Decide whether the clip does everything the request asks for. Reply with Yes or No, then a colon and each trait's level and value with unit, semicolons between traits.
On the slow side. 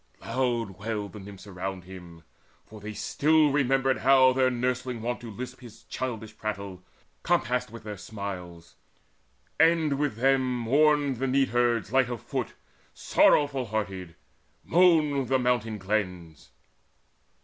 Yes: slow, 130 wpm